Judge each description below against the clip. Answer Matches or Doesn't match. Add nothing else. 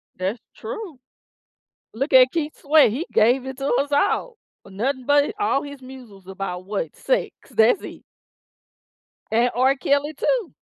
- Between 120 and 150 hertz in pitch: Doesn't match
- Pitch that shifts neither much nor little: Matches